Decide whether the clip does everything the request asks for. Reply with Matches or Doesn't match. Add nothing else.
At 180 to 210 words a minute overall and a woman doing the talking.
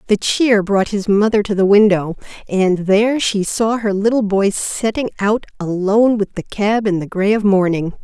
Matches